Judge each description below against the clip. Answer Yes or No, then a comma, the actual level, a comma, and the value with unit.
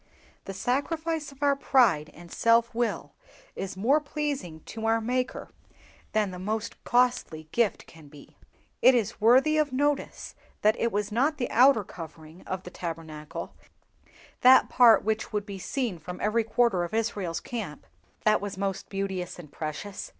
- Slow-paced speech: No, average, 160 wpm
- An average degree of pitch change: No, wide, 5.7 semitones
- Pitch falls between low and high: No, high, 215 Hz